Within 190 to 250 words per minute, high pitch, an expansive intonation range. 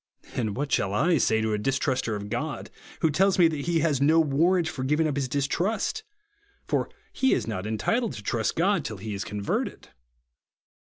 No: average, 195 wpm; medium, 140 Hz; wide, 6.8 semitones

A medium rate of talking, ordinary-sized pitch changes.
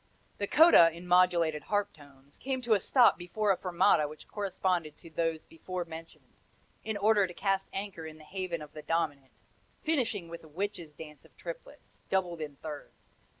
Yes: average, 180 wpm; average, 4.3 semitones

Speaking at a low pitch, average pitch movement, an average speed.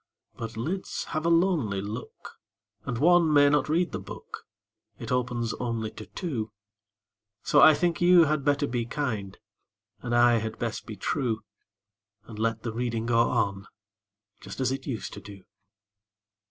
Yes: low, 120 Hz; average, 4.9 semitones; average, 160 wpm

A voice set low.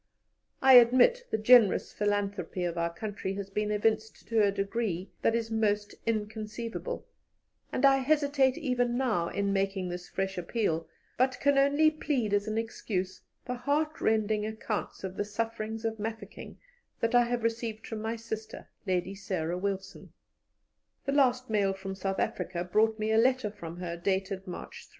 No: high, 215 Hz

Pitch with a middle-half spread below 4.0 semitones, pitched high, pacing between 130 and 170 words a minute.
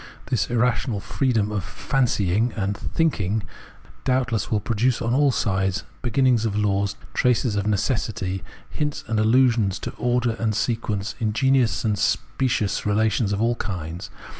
No: average, 3.4 semitones; low, 110 Hz; average, 140 wpm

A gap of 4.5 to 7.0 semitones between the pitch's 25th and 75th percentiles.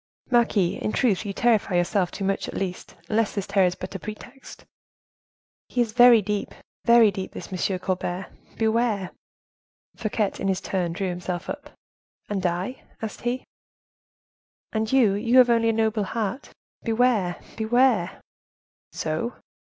No: average, 3.8 semitones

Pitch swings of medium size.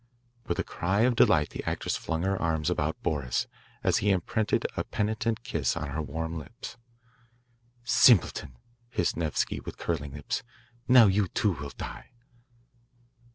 No: wide, 5.8 semitones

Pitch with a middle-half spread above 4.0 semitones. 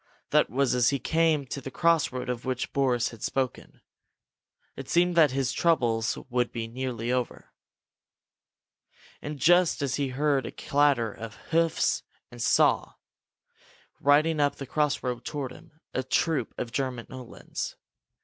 No: average, 3.3 semitones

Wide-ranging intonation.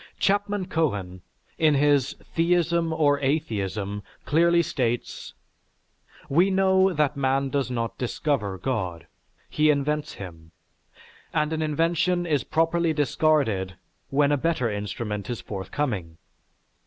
Yes: wide, 6.7 semitones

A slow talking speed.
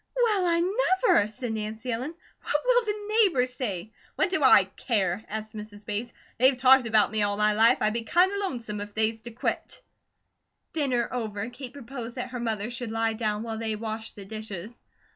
No: average, 190 wpm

